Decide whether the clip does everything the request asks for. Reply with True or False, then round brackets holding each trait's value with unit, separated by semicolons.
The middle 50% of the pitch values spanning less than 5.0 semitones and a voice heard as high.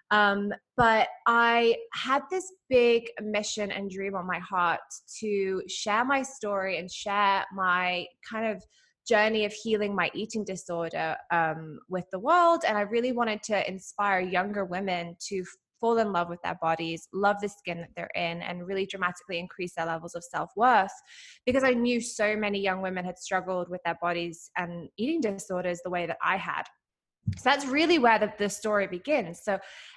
True (4.0 semitones; 200 Hz)